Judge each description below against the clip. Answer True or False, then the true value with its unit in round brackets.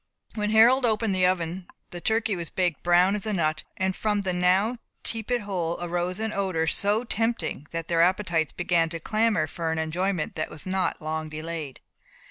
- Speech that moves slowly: False (185 wpm)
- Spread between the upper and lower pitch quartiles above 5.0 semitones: False (4.0 semitones)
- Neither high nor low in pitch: True (180 Hz)